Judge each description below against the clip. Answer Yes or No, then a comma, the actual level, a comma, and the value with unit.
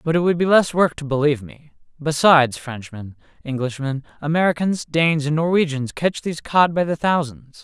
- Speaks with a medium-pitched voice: Yes, medium, 150 Hz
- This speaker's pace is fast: No, average, 175 wpm